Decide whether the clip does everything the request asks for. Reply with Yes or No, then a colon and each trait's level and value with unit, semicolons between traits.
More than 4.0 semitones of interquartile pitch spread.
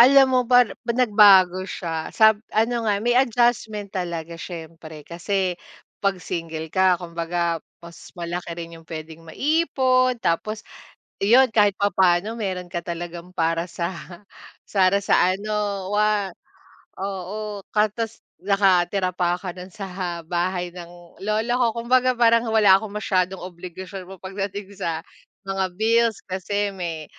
No: average, 3.6 semitones